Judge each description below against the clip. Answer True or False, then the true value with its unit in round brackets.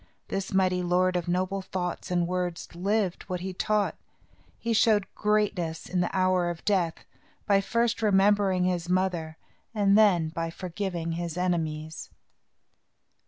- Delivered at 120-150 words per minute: True (140 wpm)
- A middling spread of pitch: False (2.2 semitones)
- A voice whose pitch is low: False (185 Hz)